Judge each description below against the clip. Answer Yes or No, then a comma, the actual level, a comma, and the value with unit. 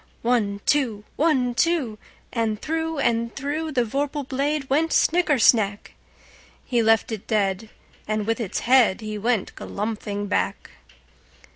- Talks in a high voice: Yes, high, 235 Hz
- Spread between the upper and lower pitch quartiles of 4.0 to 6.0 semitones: Yes, average, 4.9 semitones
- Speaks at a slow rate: Yes, slow, 120 wpm